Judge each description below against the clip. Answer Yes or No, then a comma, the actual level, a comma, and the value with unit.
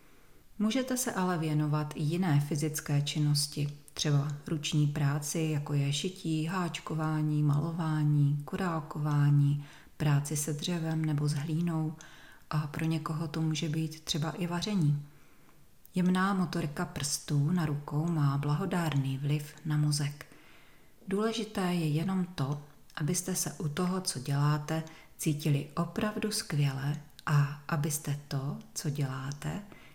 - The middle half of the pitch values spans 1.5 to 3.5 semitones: Yes, narrow, 2.5 semitones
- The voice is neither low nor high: Yes, medium, 155 Hz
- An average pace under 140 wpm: Yes, average, 120 wpm